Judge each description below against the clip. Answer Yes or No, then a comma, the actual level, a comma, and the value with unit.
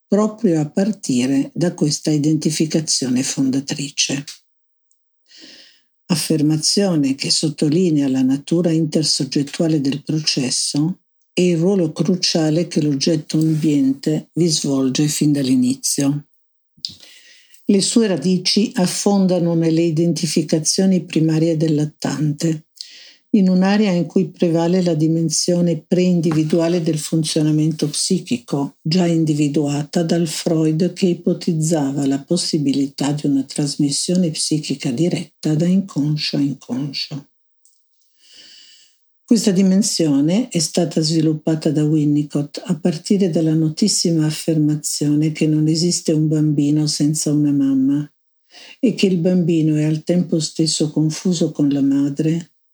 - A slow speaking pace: Yes, slow, 105 wpm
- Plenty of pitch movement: No, average, 2.9 semitones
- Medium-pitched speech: Yes, medium, 160 Hz